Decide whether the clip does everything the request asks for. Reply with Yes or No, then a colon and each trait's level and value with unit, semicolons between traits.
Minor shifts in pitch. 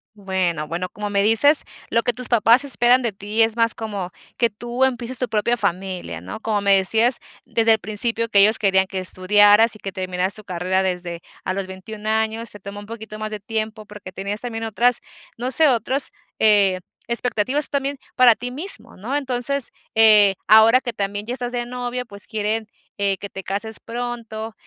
No: average, 3.3 semitones